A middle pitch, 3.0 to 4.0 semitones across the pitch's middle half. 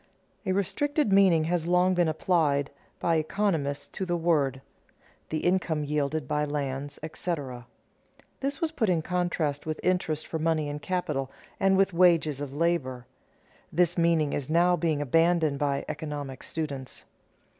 Yes: medium, 160 Hz; average, 3.5 semitones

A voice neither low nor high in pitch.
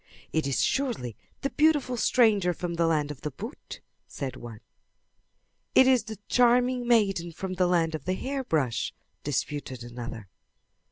Yes: medium, 175 Hz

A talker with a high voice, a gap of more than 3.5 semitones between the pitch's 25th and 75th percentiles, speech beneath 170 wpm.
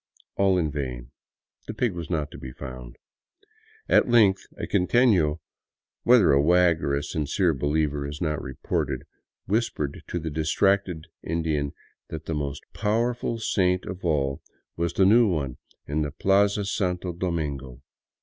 No: very low, 80 Hz; average, 4.9 semitones; average, 155 wpm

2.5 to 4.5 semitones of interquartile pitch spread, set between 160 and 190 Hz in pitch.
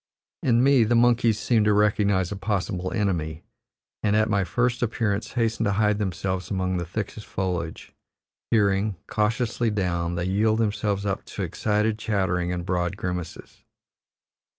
No: average, 3.0 semitones; low, 100 Hz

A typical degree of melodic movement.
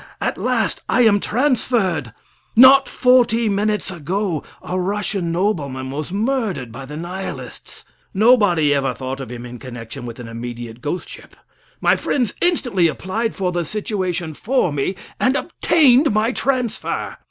No: wide, 8.2 semitones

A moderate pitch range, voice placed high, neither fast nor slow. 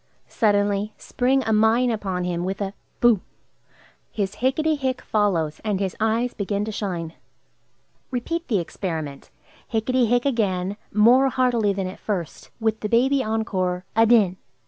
Yes: average, 4.1 semitones; high, 215 Hz; average, 145 wpm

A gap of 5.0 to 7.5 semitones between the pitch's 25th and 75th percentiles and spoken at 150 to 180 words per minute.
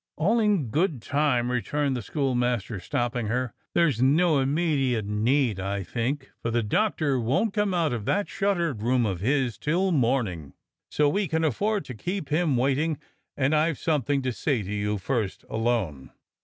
Yes: wide, 5.4 semitones; average, 170 wpm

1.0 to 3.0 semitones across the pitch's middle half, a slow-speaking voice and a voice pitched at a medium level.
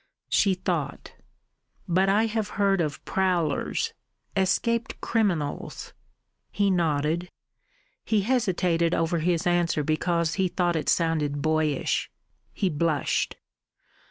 No: average, 3.5 semitones; slow, 105 wpm; medium, 175 Hz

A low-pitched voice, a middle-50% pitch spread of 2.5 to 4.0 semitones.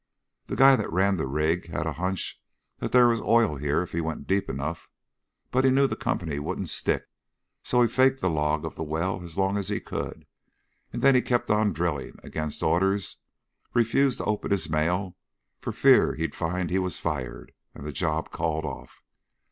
No: very low, 90 Hz; average, 5.2 semitones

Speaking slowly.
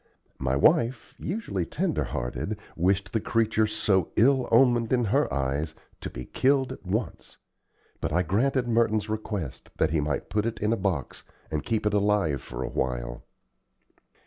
No: average, 165 wpm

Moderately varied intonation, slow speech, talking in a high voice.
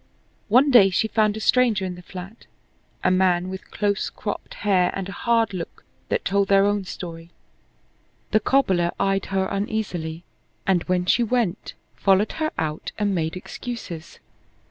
No: average, 3.2 semitones; average, 160 wpm; high, 195 Hz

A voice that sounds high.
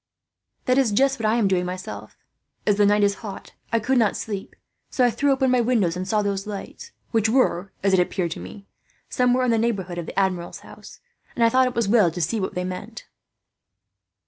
Yes: high, 210 Hz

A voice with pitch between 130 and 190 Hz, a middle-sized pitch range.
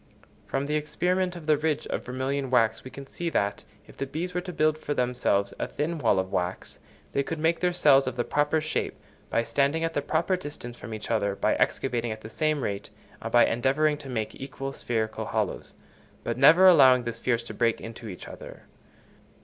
Yes: low, 135 Hz; average, 4.8 semitones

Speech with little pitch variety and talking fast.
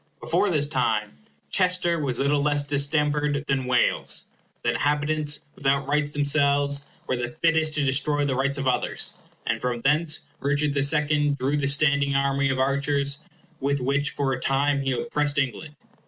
No: narrow, 1.4 semitones; average, 165 wpm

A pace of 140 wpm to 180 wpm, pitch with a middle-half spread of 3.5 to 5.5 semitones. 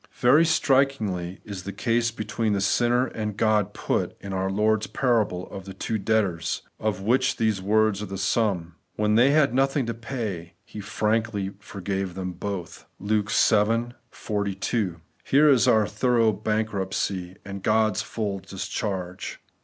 No: average, 155 wpm; average, 3.0 semitones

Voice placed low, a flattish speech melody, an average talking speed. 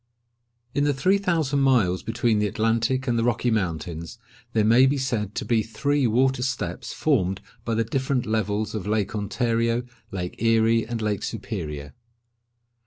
No: low, 115 Hz; average, 3.7 semitones; average, 160 wpm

